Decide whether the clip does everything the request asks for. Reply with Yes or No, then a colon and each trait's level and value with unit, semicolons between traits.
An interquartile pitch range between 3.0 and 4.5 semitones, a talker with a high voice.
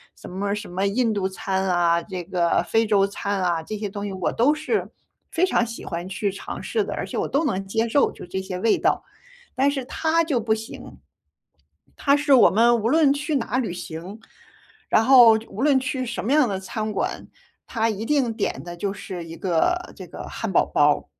No: wide, 5.4 semitones; high, 215 Hz